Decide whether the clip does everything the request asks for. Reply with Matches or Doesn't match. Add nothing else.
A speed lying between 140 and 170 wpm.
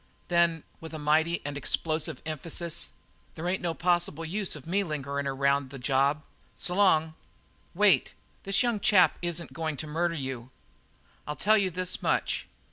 Matches